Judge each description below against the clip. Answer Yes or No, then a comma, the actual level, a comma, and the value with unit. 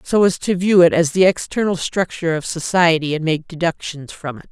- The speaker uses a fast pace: Yes, fast, 215 wpm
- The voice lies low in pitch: No, medium, 170 Hz